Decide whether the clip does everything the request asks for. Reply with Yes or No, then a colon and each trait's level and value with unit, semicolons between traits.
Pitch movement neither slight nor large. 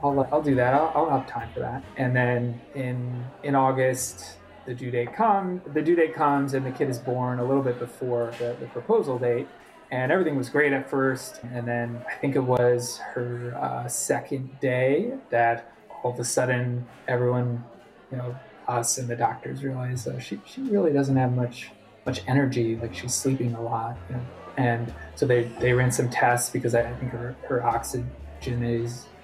No: narrow, 1.8 semitones